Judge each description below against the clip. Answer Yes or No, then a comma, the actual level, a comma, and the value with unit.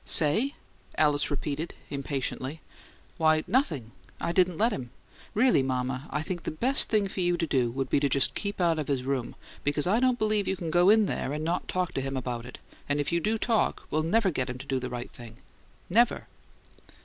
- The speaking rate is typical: No, fast, 215 wpm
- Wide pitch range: Yes, wide, 6.2 semitones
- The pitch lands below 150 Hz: No, medium, 155 Hz